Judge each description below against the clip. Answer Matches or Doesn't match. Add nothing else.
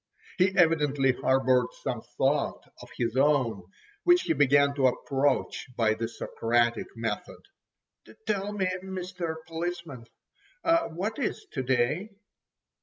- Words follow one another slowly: Matches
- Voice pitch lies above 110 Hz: Matches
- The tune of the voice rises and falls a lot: Matches